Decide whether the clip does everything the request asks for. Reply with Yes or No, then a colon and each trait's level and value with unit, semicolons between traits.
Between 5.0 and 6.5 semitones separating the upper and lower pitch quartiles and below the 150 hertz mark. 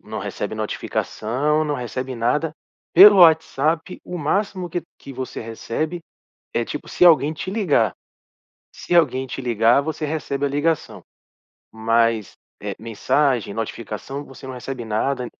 Yes: average, 5.3 semitones; medium, 140 Hz